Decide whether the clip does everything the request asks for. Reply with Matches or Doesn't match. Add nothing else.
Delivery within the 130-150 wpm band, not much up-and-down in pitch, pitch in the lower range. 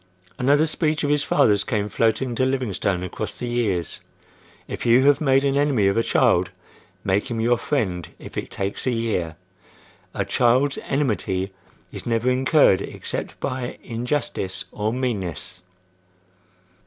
Doesn't match